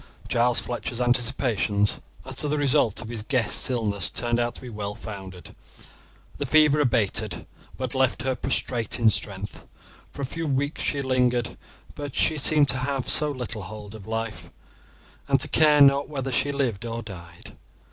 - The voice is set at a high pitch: No, low, 125 Hz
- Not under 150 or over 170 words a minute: Yes, average, 165 wpm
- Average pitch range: Yes, average, 4.1 semitones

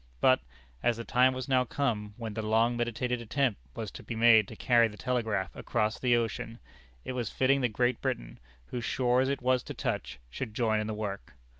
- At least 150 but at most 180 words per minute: No, fast, 205 wpm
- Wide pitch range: No, average, 2.7 semitones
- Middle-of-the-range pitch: No, low, 120 Hz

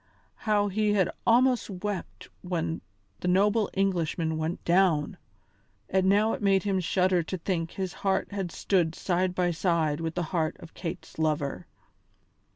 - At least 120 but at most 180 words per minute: Yes, average, 155 wpm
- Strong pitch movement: No, average, 3.1 semitones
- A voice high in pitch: No, medium, 180 Hz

